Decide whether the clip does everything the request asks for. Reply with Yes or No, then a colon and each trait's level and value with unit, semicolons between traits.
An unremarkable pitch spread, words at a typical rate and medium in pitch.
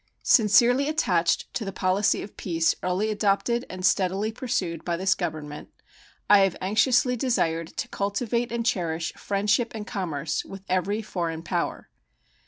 No: average, 4.5 semitones; average, 145 wpm; high, 195 Hz